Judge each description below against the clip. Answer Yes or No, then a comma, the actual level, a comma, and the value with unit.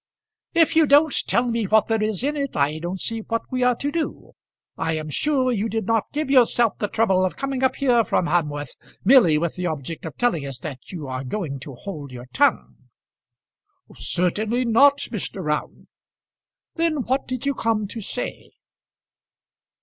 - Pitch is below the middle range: No, high, 220 Hz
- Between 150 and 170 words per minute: No, average, 180 wpm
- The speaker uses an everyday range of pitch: No, wide, 7.6 semitones